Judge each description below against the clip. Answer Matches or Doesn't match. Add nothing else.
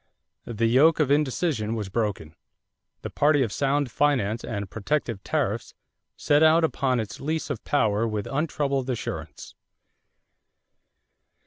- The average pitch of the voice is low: Matches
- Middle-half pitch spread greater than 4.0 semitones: Matches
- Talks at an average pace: Doesn't match